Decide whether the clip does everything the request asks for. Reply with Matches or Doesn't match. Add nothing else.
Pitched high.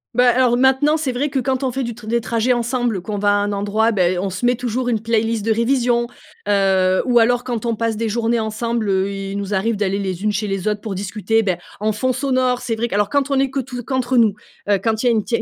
Matches